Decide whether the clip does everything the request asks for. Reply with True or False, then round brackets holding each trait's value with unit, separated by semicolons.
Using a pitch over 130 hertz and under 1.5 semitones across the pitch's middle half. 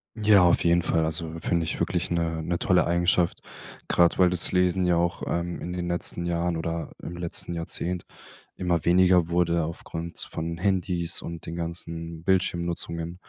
False (85 Hz; 1.1 semitones)